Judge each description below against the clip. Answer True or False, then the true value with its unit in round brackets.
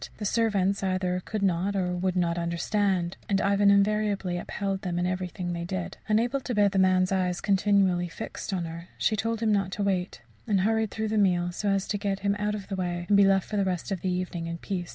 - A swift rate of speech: True (235 wpm)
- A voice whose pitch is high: True (195 Hz)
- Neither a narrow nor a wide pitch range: False (2.3 semitones)